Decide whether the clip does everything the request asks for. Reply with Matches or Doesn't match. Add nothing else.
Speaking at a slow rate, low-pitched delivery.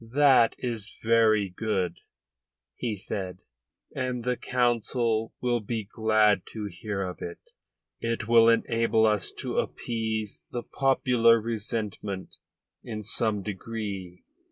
Matches